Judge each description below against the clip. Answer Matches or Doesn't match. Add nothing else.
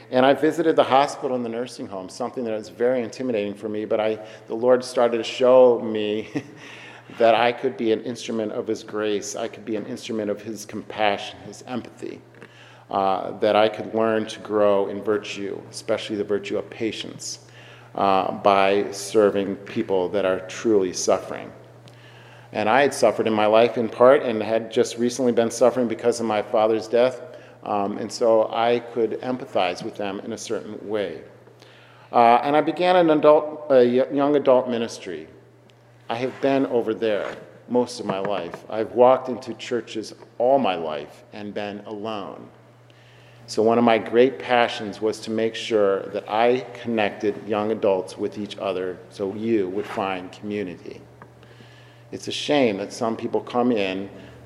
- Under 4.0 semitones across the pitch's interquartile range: Matches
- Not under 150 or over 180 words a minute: Matches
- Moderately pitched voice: Doesn't match